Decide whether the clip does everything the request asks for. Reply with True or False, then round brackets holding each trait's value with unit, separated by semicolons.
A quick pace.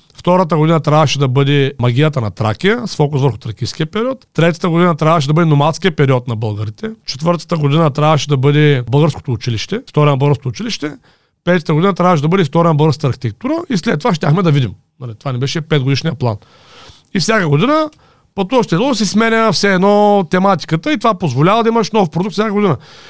True (185 wpm)